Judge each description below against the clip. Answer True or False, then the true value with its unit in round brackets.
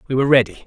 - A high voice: False (130 Hz)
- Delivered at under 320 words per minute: True (270 wpm)